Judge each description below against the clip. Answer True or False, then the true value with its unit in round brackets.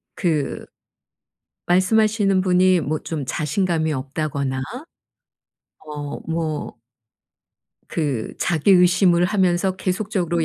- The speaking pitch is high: False (175 Hz)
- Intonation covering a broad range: False (3.4 semitones)